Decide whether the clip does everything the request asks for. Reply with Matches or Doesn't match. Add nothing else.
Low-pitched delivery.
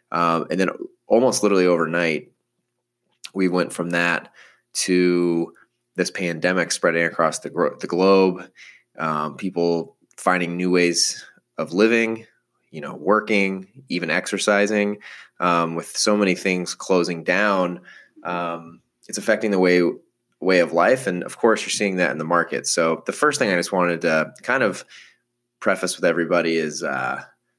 Matches